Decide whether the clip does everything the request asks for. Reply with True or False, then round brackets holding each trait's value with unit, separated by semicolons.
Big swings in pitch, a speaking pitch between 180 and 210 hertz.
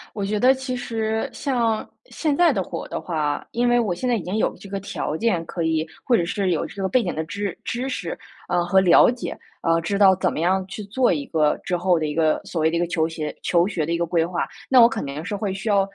False (5.0 semitones; 190 Hz)